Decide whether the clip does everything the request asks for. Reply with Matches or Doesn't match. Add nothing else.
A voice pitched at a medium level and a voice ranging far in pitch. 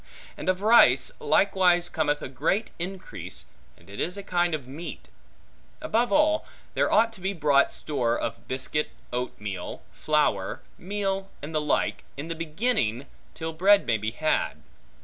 Matches